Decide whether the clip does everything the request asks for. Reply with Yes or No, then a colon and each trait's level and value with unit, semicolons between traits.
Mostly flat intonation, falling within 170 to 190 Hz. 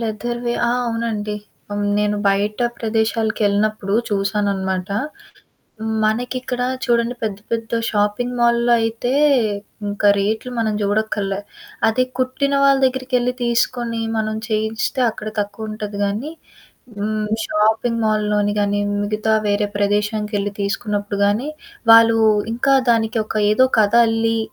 No: narrow, 2.2 semitones; high, 220 Hz